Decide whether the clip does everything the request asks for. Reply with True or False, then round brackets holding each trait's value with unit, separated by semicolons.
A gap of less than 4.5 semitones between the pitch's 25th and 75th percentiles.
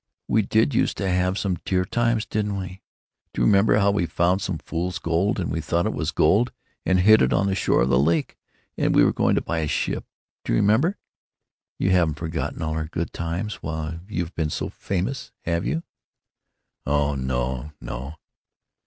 True (4.1 semitones)